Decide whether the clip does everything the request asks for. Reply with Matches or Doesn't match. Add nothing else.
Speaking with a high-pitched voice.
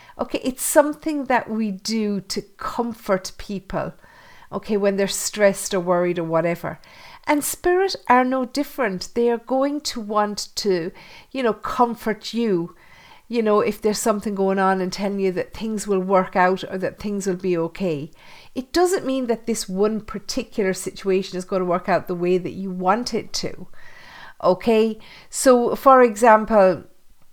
Matches